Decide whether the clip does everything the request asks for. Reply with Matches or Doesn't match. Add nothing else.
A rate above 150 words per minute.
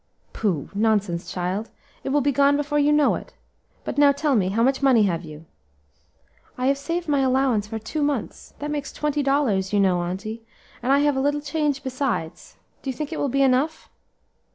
Matches